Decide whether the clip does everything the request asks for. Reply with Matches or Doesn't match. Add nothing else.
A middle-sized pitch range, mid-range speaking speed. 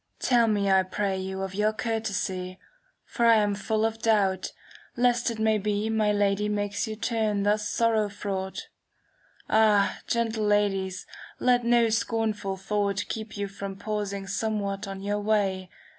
Doesn't match